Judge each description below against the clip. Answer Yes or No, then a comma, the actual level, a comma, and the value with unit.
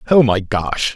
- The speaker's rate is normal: Yes, average, 190 wpm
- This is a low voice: Yes, low, 115 Hz